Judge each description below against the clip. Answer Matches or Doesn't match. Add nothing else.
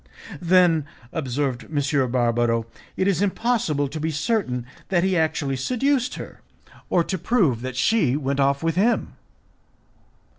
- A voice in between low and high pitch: Matches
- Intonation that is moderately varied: Doesn't match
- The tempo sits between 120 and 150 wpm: Matches